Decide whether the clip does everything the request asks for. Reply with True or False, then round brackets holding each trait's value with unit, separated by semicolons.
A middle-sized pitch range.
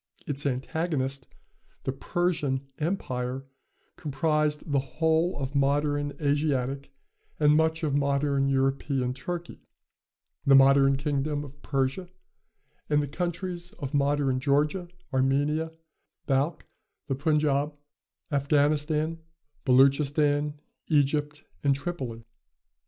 False (2.0 semitones)